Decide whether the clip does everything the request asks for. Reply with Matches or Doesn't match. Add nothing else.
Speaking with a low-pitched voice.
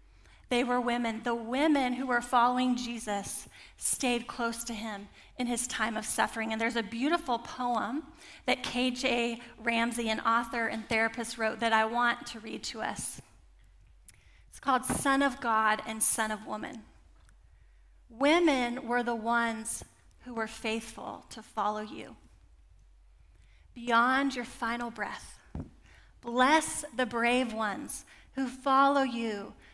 Doesn't match